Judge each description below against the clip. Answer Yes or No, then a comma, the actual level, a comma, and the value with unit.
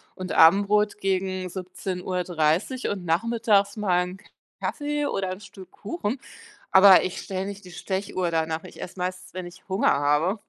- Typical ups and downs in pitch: No, narrow, 2.1 semitones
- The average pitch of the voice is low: No, high, 190 Hz